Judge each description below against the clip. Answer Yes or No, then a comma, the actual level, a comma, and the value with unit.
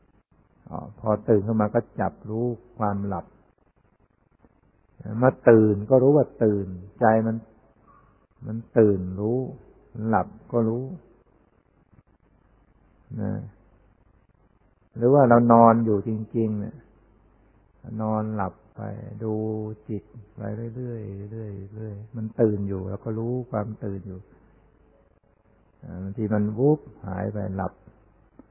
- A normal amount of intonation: No, narrow, 1.9 semitones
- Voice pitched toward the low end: Yes, low, 110 Hz